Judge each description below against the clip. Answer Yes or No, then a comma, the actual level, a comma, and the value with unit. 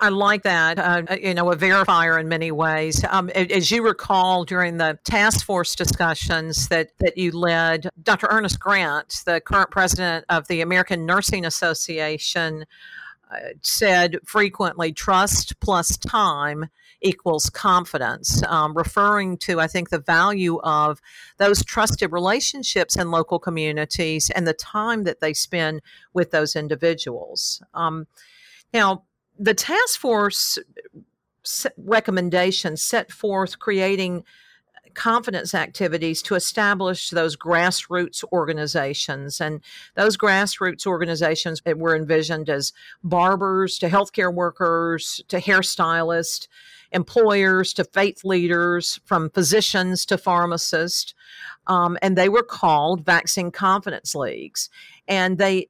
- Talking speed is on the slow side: Yes, slow, 120 wpm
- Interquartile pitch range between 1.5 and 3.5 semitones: Yes, average, 3.0 semitones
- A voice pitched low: No, medium, 180 Hz